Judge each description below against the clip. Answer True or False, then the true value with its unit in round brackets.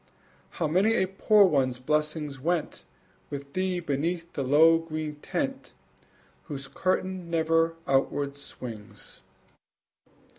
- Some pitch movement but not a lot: True (3.9 semitones)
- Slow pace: True (110 wpm)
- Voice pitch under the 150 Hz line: False (160 Hz)